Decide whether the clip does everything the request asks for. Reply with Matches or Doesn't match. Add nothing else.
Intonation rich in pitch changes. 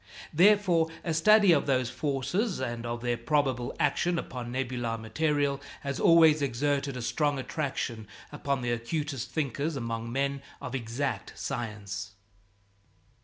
Doesn't match